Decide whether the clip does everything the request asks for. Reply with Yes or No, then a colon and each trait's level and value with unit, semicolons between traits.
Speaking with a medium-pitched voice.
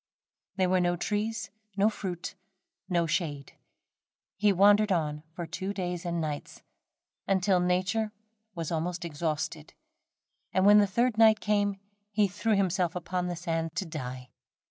Yes: medium, 180 Hz